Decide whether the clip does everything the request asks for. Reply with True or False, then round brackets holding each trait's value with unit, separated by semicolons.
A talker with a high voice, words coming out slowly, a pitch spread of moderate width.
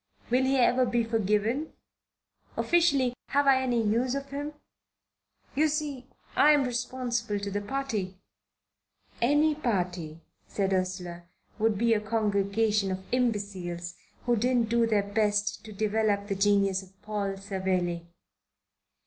True (215 Hz; 130 wpm; 4.2 semitones)